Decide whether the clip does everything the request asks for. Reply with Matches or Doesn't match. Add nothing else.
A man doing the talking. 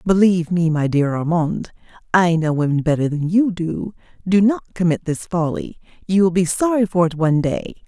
Doesn't match